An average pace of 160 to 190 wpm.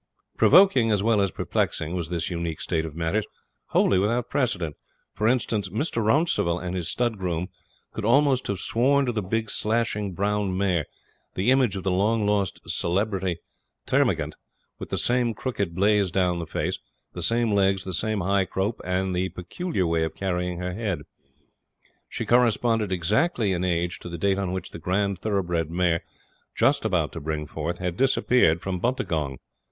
Yes: average, 170 wpm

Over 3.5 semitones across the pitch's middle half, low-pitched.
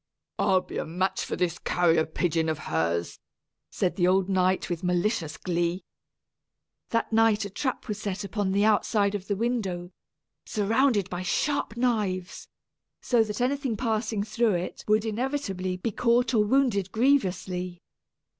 No: average, 3.9 semitones; high, 200 Hz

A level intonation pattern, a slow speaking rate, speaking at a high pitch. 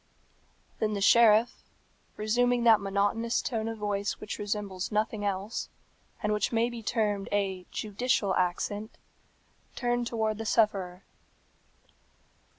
Yes: narrow, 2.2 semitones; slow, 120 wpm; high, 210 Hz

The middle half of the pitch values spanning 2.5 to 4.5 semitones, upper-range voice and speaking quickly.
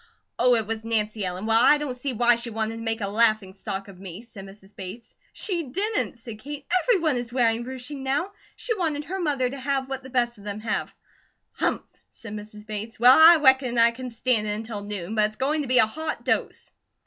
Yes: average, 3.9 semitones; high, 235 Hz; fast, 225 wpm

